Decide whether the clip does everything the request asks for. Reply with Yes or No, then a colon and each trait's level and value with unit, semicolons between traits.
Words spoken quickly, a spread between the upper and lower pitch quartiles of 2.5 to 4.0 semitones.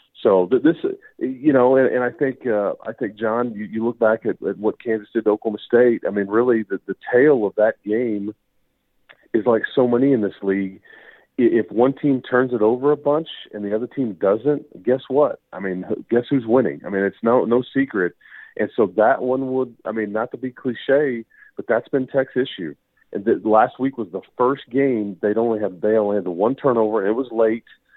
Yes: fast, 210 wpm; average, 3.6 semitones